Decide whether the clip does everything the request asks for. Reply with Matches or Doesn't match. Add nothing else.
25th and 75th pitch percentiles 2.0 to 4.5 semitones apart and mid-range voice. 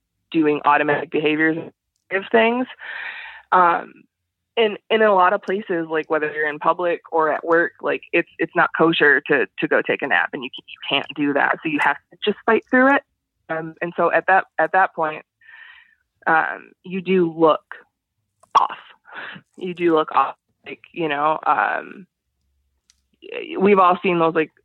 Doesn't match